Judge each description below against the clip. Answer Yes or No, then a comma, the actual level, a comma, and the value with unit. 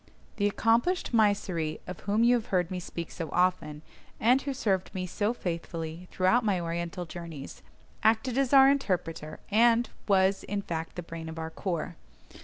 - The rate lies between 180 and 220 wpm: No, average, 170 wpm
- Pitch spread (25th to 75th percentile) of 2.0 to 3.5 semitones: No, average, 5.0 semitones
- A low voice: No, medium, 185 Hz